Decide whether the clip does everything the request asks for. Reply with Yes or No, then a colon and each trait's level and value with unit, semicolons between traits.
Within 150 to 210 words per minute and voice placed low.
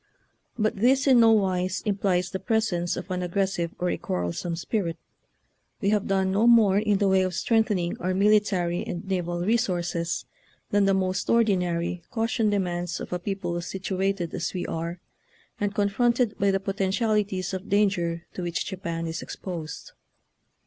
No: average, 165 wpm; high, 190 Hz